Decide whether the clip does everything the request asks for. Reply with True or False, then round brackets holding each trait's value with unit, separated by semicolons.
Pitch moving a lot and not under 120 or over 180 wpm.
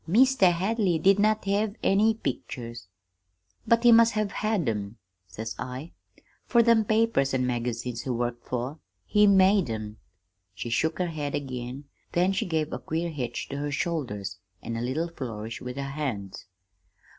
True (8.6 semitones; 165 wpm)